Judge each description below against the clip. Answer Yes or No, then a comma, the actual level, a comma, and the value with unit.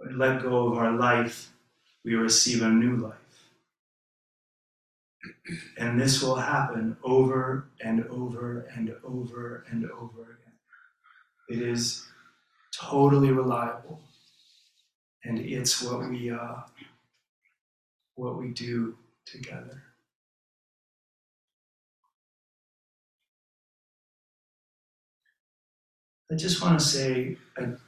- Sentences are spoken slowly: Yes, slow, 90 wpm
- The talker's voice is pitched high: No, low, 120 Hz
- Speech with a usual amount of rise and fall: No, narrow, 2.1 semitones